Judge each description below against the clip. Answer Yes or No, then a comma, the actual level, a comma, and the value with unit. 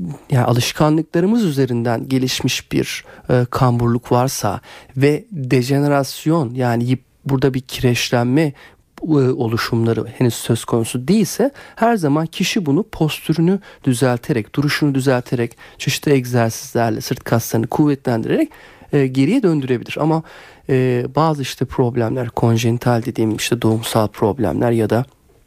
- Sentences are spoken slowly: No, average, 115 wpm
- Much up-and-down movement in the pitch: No, average, 4.0 semitones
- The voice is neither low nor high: No, low, 130 Hz